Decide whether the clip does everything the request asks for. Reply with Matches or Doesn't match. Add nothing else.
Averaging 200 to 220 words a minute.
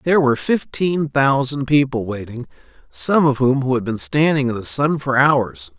Doesn't match